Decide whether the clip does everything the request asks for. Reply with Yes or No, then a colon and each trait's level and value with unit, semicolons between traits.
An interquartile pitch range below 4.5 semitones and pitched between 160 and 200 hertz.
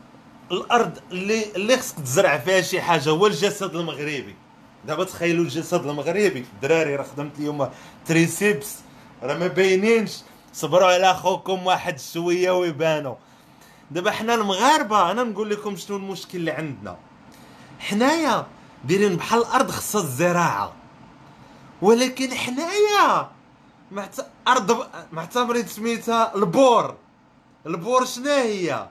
No: wide, 5.5 semitones; medium, 185 Hz